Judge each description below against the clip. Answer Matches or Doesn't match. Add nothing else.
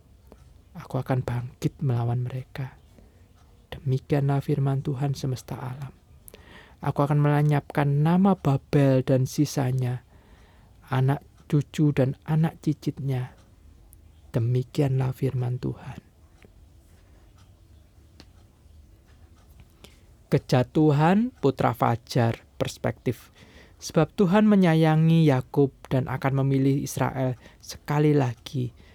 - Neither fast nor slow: Doesn't match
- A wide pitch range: Matches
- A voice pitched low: Matches